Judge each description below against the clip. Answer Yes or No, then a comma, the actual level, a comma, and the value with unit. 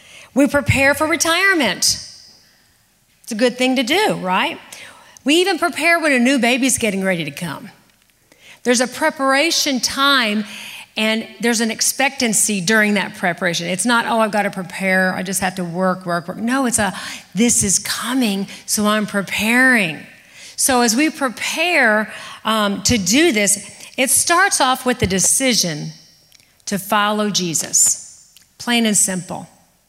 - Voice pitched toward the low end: No, high, 230 Hz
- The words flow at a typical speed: Yes, average, 155 wpm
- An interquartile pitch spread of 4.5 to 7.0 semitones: Yes, average, 4.9 semitones